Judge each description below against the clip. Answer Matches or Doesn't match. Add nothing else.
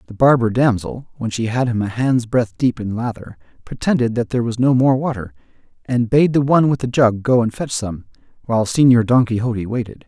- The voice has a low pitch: Matches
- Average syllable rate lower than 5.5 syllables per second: Doesn't match